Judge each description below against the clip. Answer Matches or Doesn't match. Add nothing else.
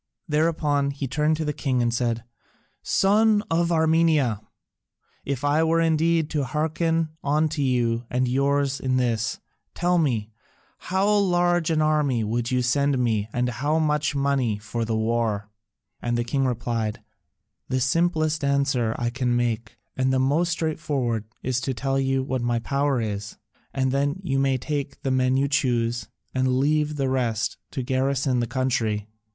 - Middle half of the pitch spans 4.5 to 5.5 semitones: Doesn't match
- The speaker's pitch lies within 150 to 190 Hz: Doesn't match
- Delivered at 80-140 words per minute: Doesn't match